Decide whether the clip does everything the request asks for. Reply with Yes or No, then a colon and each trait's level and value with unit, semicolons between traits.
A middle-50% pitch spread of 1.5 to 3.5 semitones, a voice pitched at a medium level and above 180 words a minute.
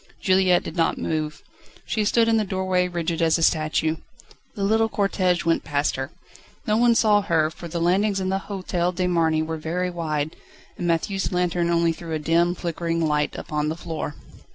Yes: average, 2.8 semitones; medium, 170 Hz; average, 190 wpm